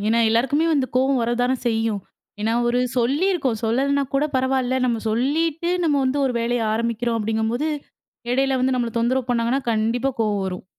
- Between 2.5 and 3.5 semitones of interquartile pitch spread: Yes, average, 2.8 semitones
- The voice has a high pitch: Yes, high, 245 Hz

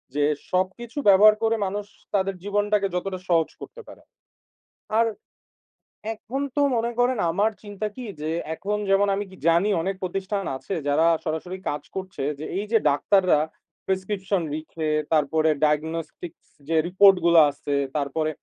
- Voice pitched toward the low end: No, high, 190 Hz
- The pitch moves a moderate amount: Yes, average, 4.3 semitones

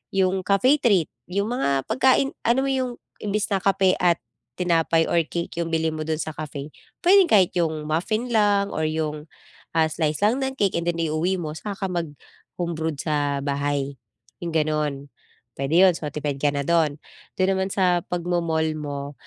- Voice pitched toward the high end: No, medium, 170 Hz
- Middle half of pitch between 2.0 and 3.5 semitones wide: No, average, 4.4 semitones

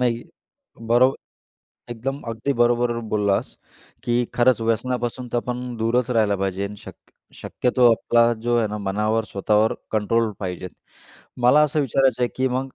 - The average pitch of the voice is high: No, low, 120 Hz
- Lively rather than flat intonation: No, narrow, 2.4 semitones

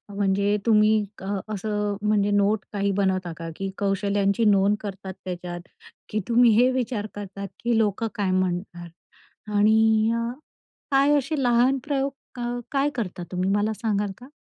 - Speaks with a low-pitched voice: No, high, 205 Hz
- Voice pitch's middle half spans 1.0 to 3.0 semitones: Yes, average, 2.7 semitones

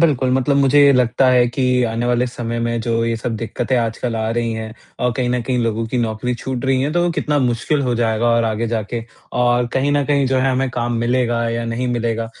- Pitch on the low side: Yes, low, 120 Hz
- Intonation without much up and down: Yes, narrow, 2.1 semitones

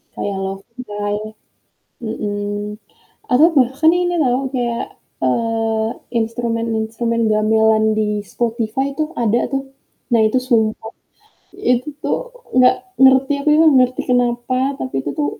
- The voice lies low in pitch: No, high, 235 Hz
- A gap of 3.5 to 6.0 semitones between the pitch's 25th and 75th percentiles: No, average, 3.1 semitones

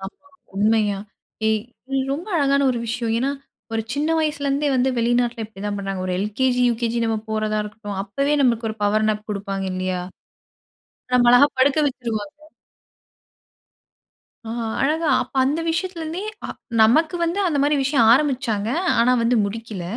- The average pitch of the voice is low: No, high, 235 Hz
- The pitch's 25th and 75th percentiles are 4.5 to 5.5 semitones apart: Yes, average, 4.9 semitones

